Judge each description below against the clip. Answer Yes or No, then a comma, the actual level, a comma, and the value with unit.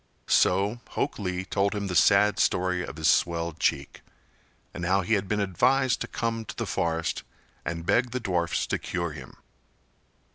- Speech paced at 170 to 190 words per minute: Yes, average, 175 wpm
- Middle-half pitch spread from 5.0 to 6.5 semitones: No, average, 3.5 semitones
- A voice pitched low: Yes, very low, 95 Hz